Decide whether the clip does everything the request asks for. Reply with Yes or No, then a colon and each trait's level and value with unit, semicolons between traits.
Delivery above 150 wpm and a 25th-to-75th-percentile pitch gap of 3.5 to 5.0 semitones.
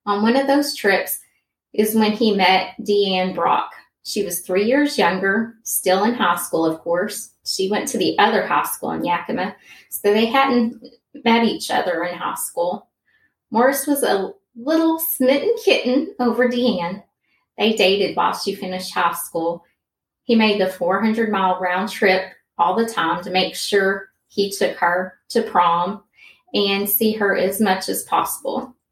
Yes: average, 165 wpm; average, 4.4 semitones